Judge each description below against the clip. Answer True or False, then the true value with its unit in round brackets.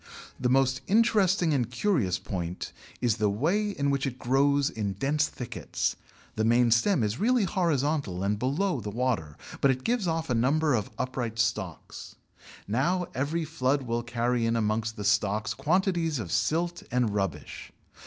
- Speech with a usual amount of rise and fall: False (6.3 semitones)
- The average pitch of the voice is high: False (130 Hz)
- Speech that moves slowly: False (165 wpm)